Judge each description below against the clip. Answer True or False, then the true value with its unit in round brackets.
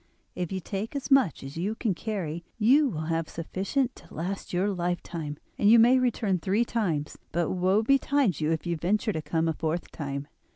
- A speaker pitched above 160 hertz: True (185 Hz)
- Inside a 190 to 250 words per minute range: True (200 wpm)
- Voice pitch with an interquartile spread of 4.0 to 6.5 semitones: True (5.4 semitones)